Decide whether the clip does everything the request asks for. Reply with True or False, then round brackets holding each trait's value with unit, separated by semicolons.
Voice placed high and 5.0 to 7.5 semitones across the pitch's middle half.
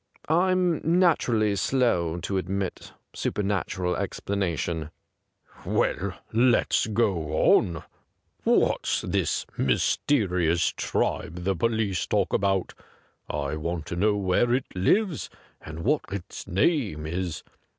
False (95 Hz; 5.5 semitones)